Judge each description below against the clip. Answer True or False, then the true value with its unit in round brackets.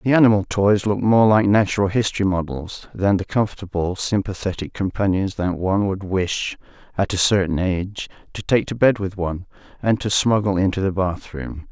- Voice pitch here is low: True (100 Hz)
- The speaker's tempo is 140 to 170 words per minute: False (180 wpm)